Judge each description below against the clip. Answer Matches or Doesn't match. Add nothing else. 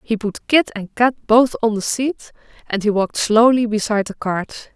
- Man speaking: Doesn't match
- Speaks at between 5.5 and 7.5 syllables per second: Doesn't match